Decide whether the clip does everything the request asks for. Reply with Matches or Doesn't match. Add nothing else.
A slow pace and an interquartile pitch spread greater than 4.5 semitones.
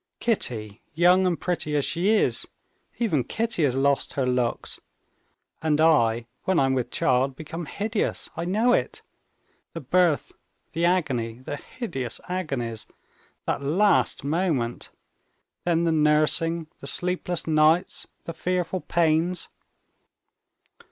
Matches